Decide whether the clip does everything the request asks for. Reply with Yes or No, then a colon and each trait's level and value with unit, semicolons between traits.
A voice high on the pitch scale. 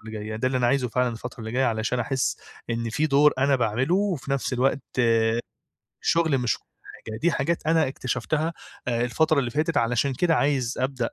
No: low, 130 Hz